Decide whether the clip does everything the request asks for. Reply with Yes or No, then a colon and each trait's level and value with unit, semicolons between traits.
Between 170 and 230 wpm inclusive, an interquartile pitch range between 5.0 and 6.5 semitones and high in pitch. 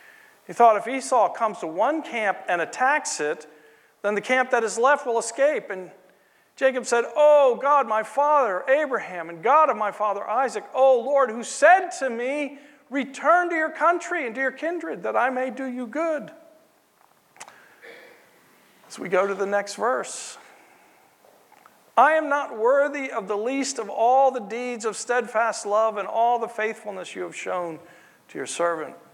Yes: average, 175 wpm; average, 5.3 semitones; very high, 250 Hz